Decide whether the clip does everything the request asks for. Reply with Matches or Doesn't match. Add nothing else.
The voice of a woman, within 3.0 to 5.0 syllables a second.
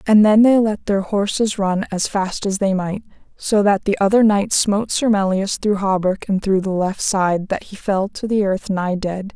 Matches